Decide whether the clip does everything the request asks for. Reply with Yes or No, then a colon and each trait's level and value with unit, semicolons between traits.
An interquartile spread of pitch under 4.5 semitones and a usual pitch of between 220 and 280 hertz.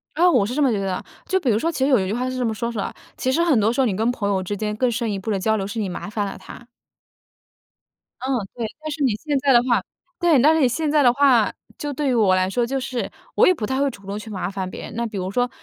No: average, 4.8 semitones; high, 235 Hz